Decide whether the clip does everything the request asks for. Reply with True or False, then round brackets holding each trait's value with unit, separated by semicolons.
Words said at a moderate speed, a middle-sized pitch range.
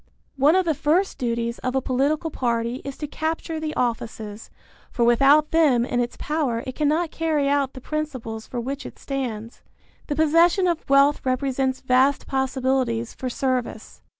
True (165 wpm; 3.9 semitones)